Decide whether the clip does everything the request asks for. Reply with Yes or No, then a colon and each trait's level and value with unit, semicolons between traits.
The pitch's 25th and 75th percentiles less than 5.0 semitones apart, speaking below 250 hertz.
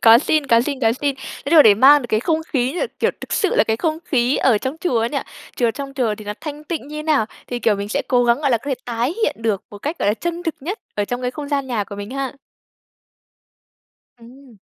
No: average, 4.4 semitones; very high, 260 Hz